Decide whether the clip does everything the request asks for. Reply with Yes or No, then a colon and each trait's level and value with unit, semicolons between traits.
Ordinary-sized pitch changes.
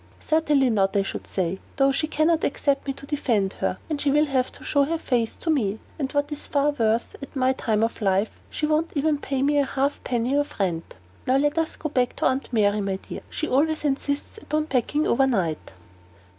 Yes: average, 4.6 semitones